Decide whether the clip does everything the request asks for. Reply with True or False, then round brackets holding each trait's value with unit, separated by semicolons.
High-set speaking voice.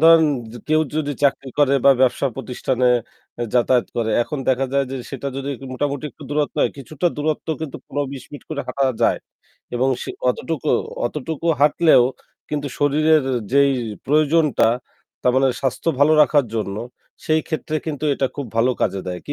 False (140 Hz)